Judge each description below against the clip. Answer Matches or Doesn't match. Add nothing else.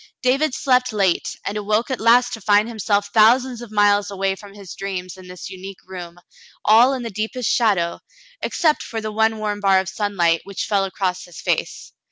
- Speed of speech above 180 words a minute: Matches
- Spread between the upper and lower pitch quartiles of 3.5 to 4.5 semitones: Doesn't match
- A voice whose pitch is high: Matches